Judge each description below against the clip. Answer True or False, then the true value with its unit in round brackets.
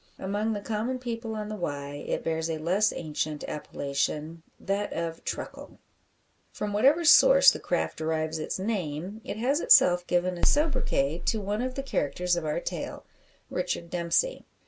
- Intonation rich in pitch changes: True (6.0 semitones)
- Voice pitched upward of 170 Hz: True (185 Hz)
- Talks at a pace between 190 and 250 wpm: False (165 wpm)